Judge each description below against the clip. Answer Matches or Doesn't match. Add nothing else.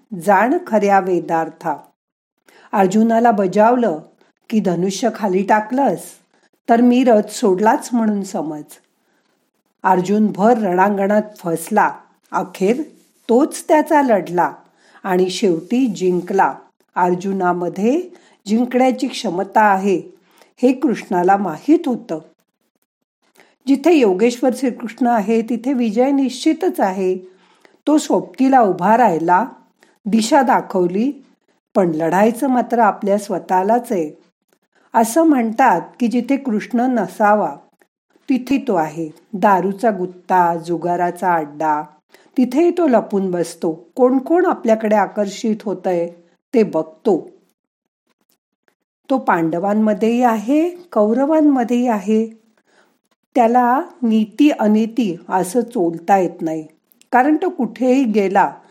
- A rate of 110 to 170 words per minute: Doesn't match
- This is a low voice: Doesn't match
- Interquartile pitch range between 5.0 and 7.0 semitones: Matches